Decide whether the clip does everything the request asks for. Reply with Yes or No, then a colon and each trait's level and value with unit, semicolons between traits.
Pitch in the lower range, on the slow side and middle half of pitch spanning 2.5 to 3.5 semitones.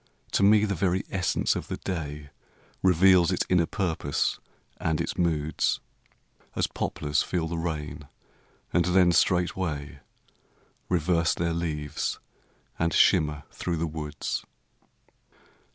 Yes: very low, 85 Hz; slow, 120 wpm; average, 3.1 semitones